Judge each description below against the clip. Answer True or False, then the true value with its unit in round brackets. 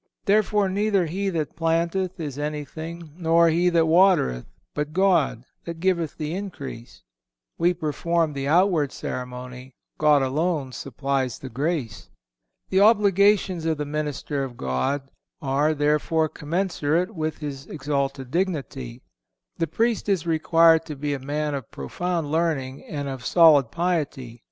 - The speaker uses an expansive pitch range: False (3.9 semitones)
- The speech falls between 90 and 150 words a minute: True (135 wpm)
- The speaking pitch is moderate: True (155 Hz)